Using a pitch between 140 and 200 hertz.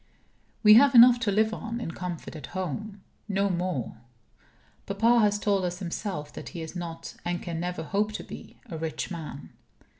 Yes: medium, 185 Hz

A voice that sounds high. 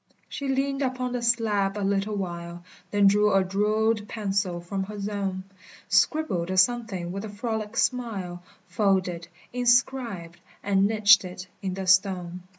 Yes: high, 200 Hz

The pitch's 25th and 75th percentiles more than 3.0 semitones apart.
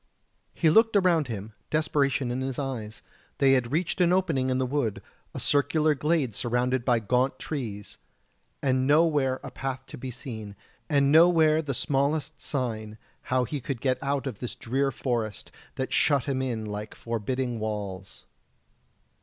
Yes: average, 3.6 semitones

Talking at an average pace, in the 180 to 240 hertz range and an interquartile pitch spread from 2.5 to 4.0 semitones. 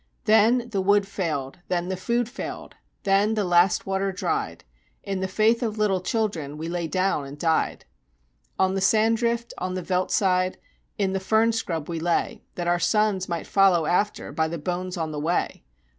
Yes: average, 190 wpm; high, 190 Hz; average, 3.5 semitones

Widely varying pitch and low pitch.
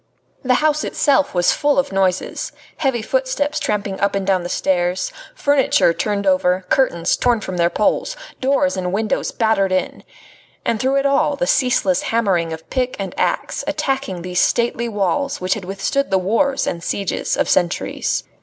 No: wide, 6.5 semitones; high, 210 Hz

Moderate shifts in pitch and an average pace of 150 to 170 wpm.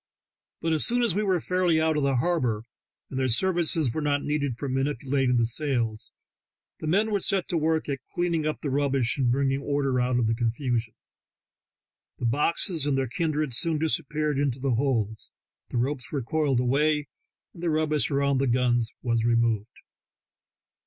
No: average, 4.1 semitones; average, 180 wpm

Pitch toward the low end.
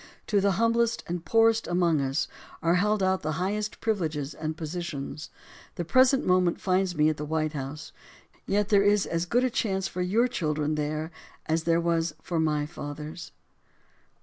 No: medium, 170 Hz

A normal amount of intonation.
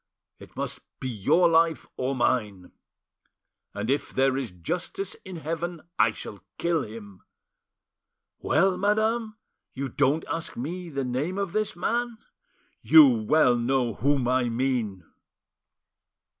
No: wide, 6.4 semitones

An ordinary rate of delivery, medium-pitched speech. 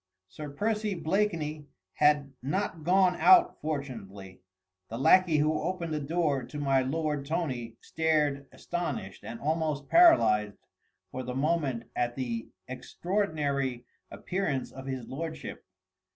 No: slow, 125 wpm; medium, 150 Hz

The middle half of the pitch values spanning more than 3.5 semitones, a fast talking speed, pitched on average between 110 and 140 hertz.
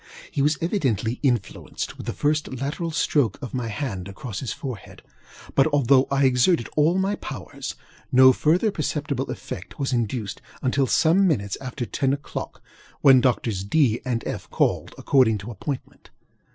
No: average, 3.9 semitones; average, 155 wpm; low, 135 Hz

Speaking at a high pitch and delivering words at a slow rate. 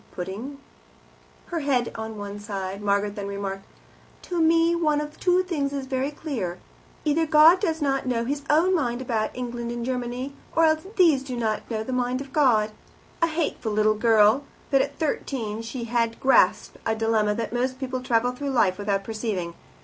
No: high, 245 Hz; average, 180 wpm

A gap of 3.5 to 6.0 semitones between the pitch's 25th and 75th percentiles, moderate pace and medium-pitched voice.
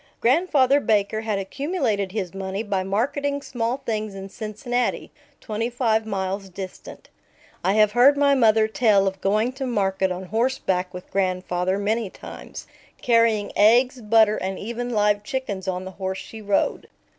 No: average, 3.8 semitones; average, 155 wpm; high, 215 Hz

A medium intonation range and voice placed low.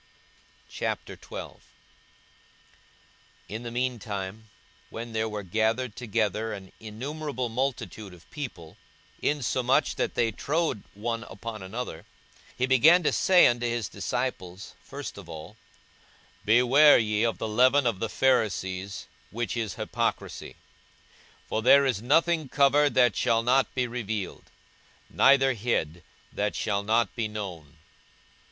Yes: average, 3.7 semitones; low, 115 Hz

